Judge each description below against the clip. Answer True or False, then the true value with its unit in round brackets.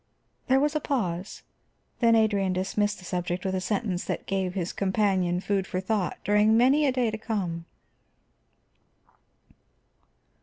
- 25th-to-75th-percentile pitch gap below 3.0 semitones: False (3.3 semitones)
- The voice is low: False (200 Hz)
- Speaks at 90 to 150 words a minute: True (145 wpm)